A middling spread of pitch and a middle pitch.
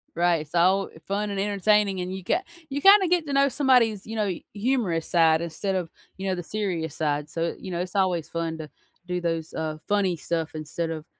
Yes: average, 4.0 semitones; medium, 180 Hz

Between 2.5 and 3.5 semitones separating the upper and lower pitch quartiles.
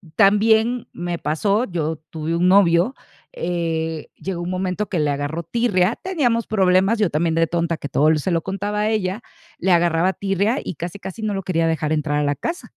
No: average, 4.0 semitones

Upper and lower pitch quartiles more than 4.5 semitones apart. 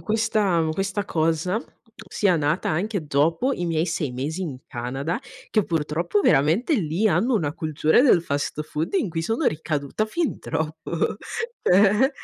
Yes: average, 5.0 semitones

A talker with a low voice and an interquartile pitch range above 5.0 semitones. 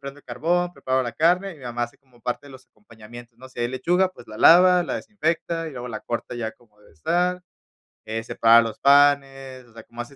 Yes: low, 130 Hz; wide, 5.6 semitones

